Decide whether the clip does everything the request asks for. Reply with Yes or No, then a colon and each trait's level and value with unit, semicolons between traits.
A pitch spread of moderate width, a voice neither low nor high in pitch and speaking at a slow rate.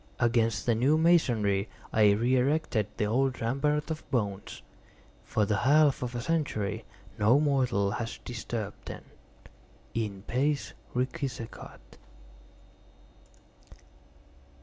No: average, 4.4 semitones; low, 120 Hz; slow, 105 wpm